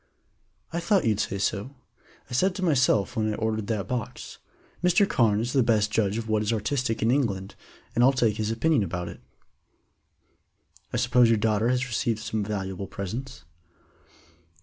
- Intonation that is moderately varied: Yes, average, 3.4 semitones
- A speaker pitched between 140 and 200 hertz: No, low, 110 Hz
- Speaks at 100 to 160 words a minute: No, average, 170 wpm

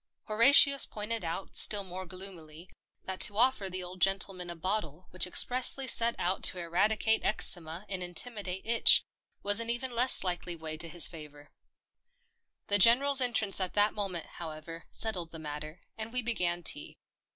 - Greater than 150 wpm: Yes, average, 165 wpm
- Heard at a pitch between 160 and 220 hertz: Yes, high, 190 Hz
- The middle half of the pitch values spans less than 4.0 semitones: No, average, 4.4 semitones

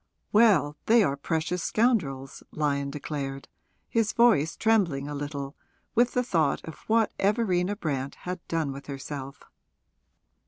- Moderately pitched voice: Yes, medium, 160 Hz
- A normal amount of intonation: No, wide, 7.2 semitones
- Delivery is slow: Yes, slow, 130 wpm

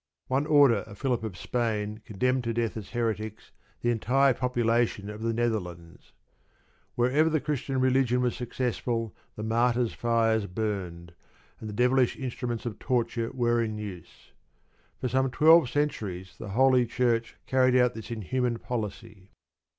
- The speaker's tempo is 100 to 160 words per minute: Yes, average, 145 wpm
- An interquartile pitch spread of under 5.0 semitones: Yes, average, 2.8 semitones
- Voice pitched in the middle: No, low, 120 Hz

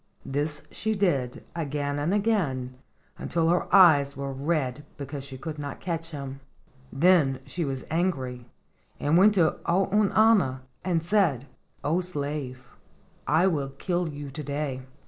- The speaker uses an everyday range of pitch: Yes, average, 4.3 semitones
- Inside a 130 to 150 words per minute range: Yes, average, 140 wpm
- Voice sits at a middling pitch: Yes, medium, 150 Hz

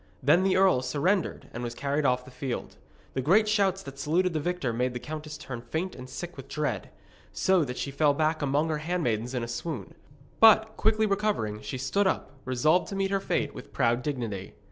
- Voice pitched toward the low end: No, medium, 150 Hz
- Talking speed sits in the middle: No, fast, 210 wpm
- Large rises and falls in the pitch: Yes, wide, 6.5 semitones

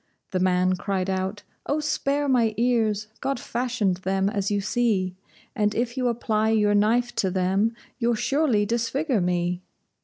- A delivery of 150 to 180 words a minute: Yes, average, 155 wpm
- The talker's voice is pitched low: No, high, 215 Hz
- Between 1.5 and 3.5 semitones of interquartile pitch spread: No, average, 4.0 semitones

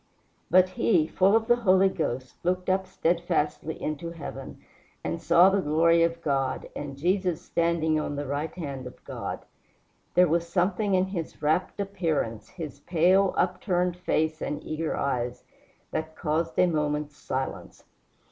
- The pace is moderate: Yes, average, 150 wpm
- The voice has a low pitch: No, medium, 170 Hz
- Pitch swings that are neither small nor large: Yes, average, 3.3 semitones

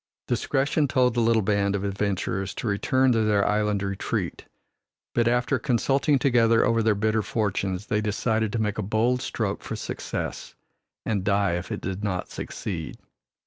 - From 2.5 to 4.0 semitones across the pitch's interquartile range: Yes, average, 3.0 semitones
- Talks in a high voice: No, low, 110 Hz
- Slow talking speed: No, average, 165 wpm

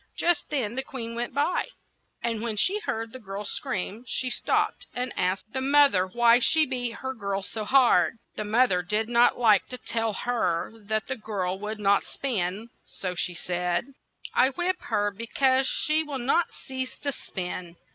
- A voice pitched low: No, high, 230 Hz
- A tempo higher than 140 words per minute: Yes, average, 185 wpm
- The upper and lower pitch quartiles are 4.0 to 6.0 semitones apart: Yes, average, 4.6 semitones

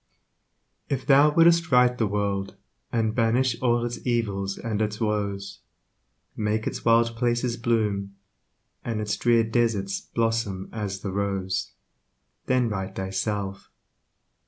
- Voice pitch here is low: Yes, low, 110 Hz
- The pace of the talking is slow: Yes, slow, 125 wpm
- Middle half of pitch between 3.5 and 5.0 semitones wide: No, average, 3.0 semitones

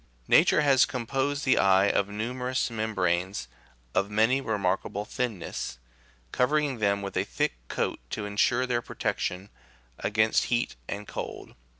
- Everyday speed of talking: No, slow, 130 wpm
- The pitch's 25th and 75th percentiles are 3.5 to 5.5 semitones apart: Yes, average, 3.9 semitones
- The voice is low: Yes, low, 110 Hz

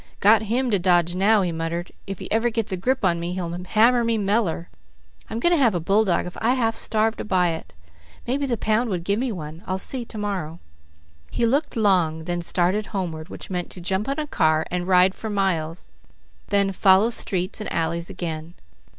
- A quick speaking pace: Yes, fast, 210 wpm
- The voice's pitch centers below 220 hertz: Yes, high, 190 Hz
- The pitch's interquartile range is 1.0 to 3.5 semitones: No, average, 4.3 semitones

